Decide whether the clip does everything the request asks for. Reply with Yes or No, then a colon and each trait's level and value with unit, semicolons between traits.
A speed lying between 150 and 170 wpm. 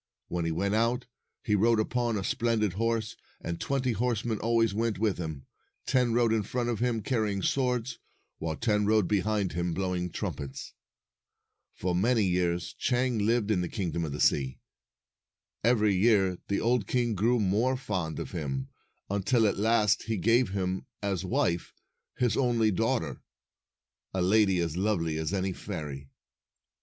Yes: average, 160 wpm